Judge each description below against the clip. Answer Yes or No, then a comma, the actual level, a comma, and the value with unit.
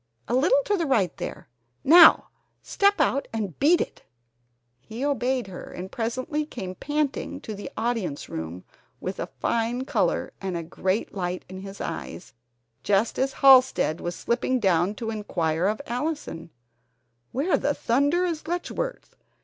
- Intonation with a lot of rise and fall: Yes, wide, 7.2 semitones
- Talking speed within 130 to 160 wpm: Yes, average, 150 wpm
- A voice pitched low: No, high, 235 Hz